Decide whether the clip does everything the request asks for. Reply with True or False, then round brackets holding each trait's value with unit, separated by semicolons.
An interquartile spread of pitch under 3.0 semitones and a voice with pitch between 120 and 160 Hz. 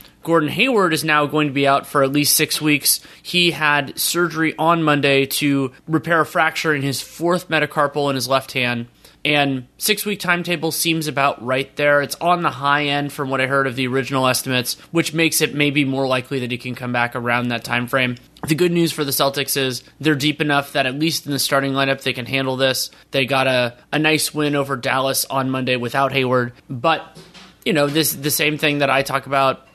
True (2.6 semitones; 140 Hz)